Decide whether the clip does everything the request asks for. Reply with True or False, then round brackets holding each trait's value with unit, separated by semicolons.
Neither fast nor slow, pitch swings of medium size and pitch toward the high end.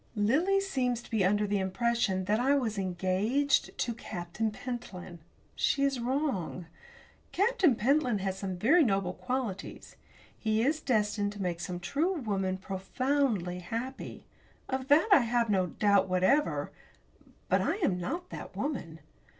False (145 wpm; 6.3 semitones; 220 Hz)